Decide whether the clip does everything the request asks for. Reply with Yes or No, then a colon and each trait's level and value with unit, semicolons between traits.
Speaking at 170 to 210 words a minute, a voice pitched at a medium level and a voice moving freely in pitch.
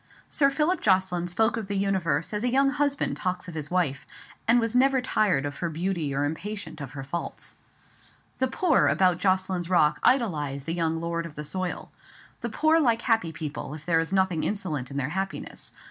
Yes: average, 195 wpm; medium, 180 Hz; wide, 6.0 semitones